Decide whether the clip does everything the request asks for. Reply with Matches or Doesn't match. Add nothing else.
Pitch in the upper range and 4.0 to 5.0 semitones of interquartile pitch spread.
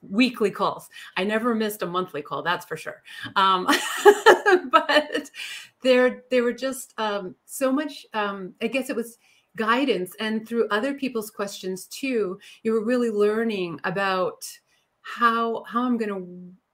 Matches